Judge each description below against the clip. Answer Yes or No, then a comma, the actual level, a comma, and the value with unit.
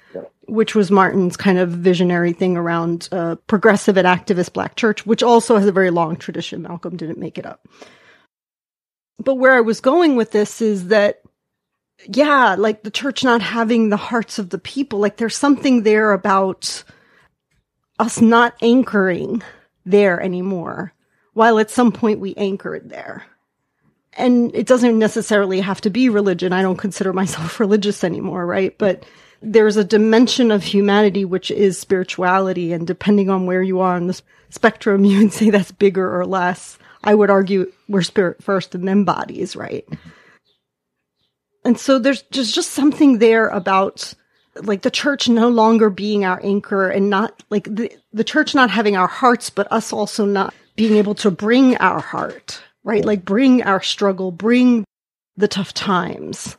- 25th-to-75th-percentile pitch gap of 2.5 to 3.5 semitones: Yes, average, 3.2 semitones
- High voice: Yes, high, 205 Hz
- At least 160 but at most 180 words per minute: Yes, average, 170 wpm